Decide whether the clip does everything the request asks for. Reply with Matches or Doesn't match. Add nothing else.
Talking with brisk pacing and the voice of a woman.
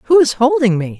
Matches